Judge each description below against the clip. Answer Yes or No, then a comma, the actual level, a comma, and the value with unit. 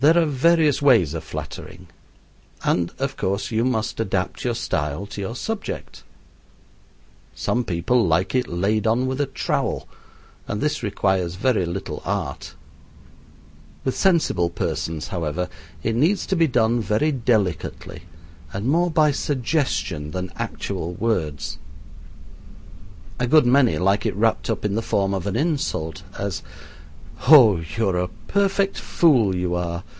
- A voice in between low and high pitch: No, low, 105 Hz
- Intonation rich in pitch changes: Yes, wide, 6.8 semitones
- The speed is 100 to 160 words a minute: Yes, average, 145 wpm